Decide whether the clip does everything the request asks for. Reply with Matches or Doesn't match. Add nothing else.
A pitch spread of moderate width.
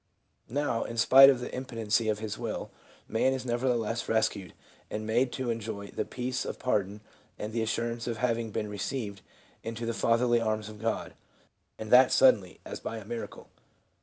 Doesn't match